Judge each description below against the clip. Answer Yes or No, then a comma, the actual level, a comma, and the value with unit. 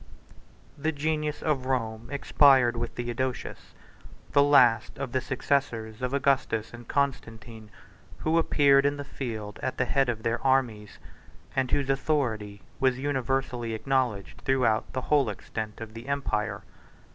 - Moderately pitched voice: No, low, 130 Hz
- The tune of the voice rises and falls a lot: No, average, 3.5 semitones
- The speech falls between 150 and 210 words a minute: No, average, 140 wpm